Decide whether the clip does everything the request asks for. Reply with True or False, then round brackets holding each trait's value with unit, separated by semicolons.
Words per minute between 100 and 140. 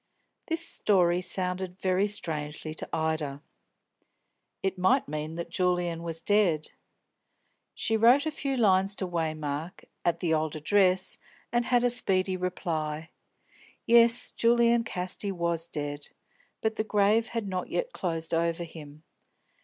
True (135 wpm)